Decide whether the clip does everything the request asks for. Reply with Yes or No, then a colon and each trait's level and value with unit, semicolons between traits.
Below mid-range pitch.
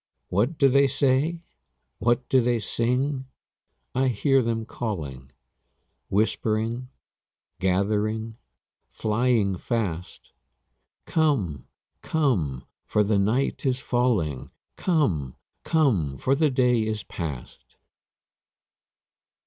Yes: low, 115 Hz